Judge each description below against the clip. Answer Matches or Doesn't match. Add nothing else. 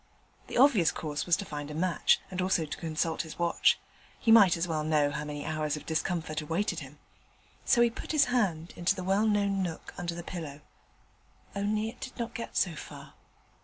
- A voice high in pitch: Doesn't match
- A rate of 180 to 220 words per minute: Matches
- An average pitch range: Matches